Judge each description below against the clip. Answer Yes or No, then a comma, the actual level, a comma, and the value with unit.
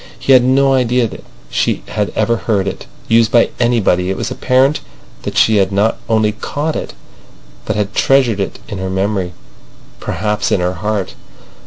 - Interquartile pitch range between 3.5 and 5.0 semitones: Yes, average, 3.9 semitones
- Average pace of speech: Yes, average, 170 wpm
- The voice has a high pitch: No, low, 110 Hz